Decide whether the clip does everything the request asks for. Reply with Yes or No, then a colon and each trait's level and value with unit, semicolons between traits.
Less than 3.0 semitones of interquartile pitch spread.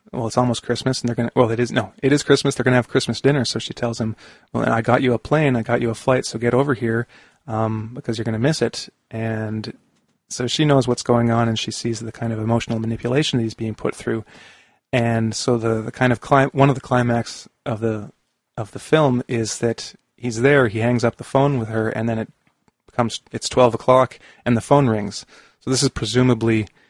Yes: narrow, 2.5 semitones